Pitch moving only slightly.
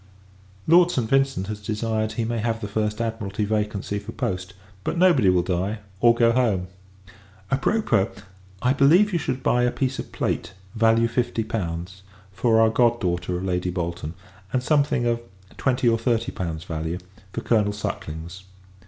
No: average, 4.4 semitones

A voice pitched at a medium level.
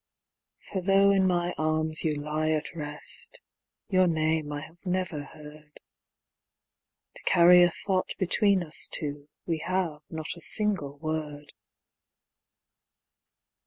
Yes: medium, 160 Hz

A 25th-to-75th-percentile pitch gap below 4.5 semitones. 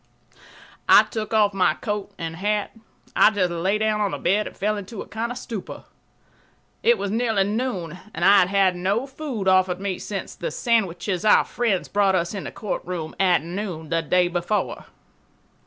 Yes: average, 2.9 semitones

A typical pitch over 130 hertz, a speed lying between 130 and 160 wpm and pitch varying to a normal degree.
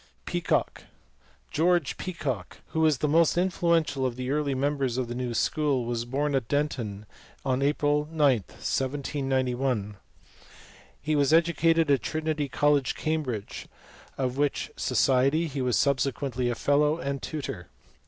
Yes: medium, 140 Hz; average, 140 wpm; average, 3.0 semitones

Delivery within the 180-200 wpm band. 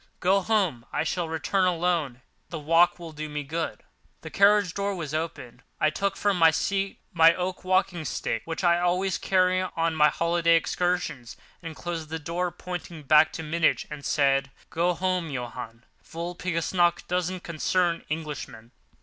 No: average, 155 wpm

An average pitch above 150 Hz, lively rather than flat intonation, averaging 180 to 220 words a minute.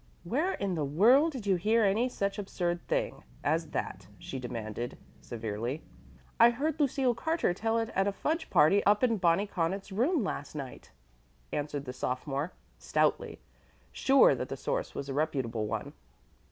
No: high, 190 Hz; wide, 8.7 semitones; average, 165 wpm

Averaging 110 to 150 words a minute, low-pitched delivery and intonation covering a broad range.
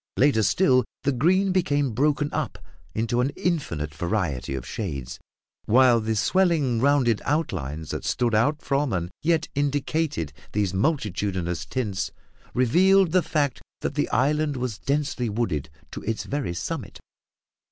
Yes: average, 140 wpm; low, 125 Hz; wide, 6.8 semitones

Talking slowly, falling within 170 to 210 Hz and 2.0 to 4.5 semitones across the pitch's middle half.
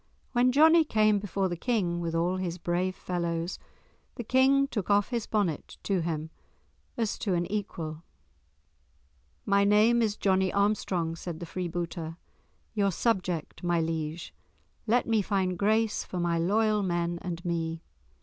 No: average, 150 wpm; medium, 185 Hz; average, 3.8 semitones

